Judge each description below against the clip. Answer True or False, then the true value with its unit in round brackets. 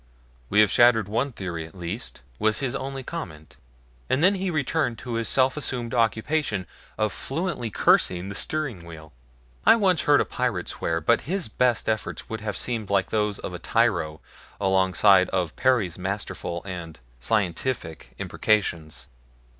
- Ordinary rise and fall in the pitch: False (6.2 semitones)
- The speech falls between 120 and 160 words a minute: True (155 wpm)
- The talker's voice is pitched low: True (110 Hz)